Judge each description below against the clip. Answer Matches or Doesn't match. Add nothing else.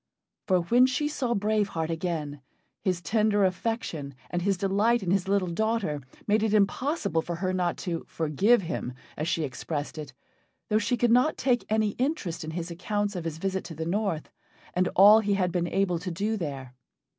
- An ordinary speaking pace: Matches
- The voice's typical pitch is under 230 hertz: Matches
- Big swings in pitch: Doesn't match